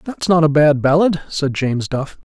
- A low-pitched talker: No, medium, 155 Hz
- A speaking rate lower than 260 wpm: Yes, average, 200 wpm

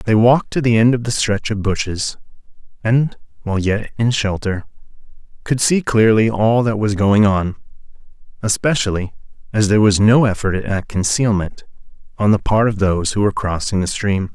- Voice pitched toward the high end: No, low, 110 Hz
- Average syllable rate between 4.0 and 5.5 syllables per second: Yes, 5.2 syllables/s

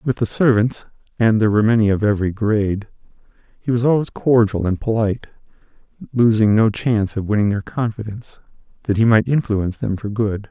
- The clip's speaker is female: No, male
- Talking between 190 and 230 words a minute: No, average, 170 wpm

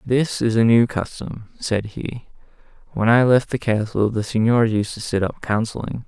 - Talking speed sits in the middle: Yes, average, 190 wpm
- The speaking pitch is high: No, low, 115 Hz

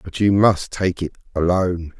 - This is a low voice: Yes, very low, 90 Hz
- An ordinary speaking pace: Yes, average, 180 wpm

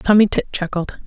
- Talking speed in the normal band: Yes, average, 170 wpm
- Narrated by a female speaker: Yes, female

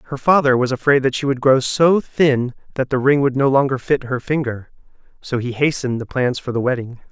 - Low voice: Yes, low, 130 Hz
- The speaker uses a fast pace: Yes, fast, 230 wpm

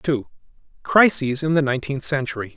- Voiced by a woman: No, male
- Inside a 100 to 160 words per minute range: Yes, average, 140 wpm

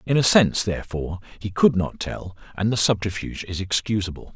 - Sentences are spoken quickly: No, average, 180 wpm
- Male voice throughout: Yes, male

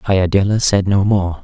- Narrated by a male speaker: Yes, male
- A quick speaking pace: No, average, 170 wpm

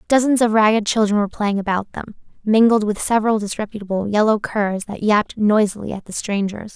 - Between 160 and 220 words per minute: Yes, average, 180 wpm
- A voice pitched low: No, high, 210 Hz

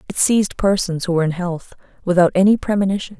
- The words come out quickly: No, average, 190 wpm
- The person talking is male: No, female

